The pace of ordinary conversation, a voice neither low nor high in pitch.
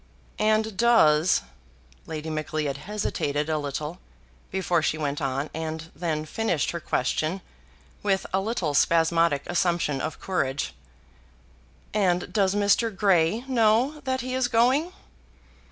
No: slow, 125 wpm; medium, 170 Hz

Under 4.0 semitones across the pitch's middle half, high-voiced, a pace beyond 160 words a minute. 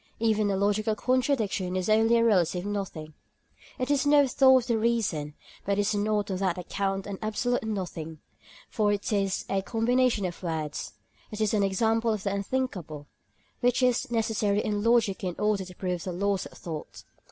Yes: average, 3.2 semitones; high, 205 Hz; average, 185 wpm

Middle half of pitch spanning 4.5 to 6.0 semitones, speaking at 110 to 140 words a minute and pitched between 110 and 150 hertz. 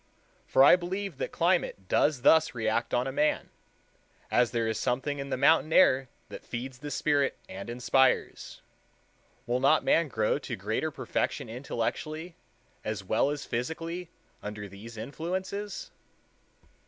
Yes: wide, 5.4 semitones; slow, 135 wpm; low, 135 Hz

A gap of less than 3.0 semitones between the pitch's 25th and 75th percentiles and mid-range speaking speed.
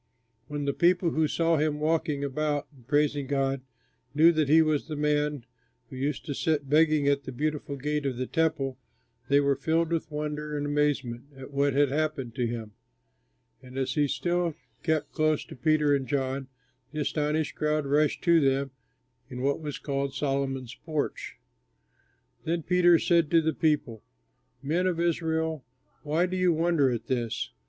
Yes: narrow, 2.5 semitones; average, 170 wpm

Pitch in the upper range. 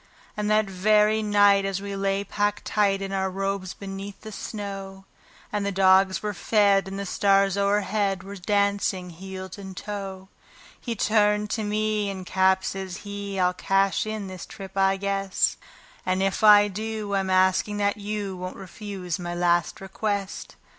Yes: high, 195 Hz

